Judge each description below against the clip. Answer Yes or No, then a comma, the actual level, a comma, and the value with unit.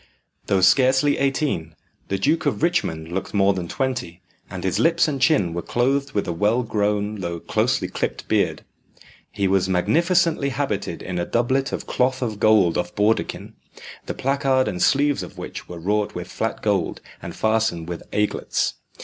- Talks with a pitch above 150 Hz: No, low, 105 Hz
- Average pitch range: No, wide, 6.6 semitones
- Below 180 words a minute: Yes, average, 170 wpm